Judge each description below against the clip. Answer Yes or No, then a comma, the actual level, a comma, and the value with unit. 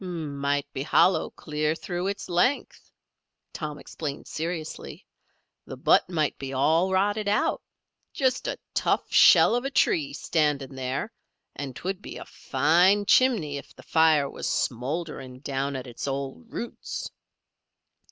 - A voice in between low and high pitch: Yes, medium, 160 Hz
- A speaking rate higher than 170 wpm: No, average, 140 wpm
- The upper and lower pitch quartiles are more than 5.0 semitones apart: Yes, wide, 5.5 semitones